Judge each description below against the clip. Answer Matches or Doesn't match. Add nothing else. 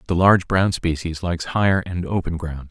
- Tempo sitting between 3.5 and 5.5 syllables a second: Doesn't match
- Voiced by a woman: Doesn't match